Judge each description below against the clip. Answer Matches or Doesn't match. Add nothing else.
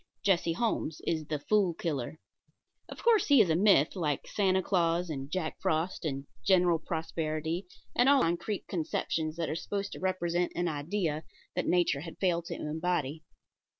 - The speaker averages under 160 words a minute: Doesn't match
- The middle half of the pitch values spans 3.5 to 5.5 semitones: Doesn't match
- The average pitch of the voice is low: Doesn't match